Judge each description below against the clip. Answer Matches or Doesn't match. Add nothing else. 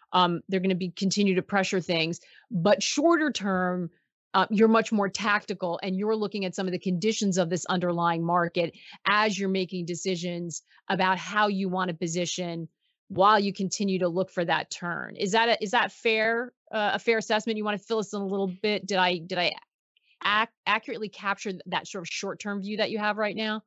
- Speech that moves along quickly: Matches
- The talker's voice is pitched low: Doesn't match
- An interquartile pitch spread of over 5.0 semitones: Doesn't match